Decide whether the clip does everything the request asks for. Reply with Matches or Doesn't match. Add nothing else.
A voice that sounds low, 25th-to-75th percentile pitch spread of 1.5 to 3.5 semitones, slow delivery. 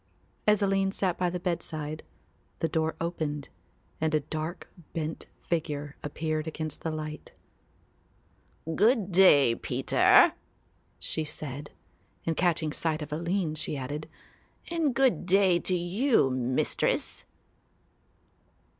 Doesn't match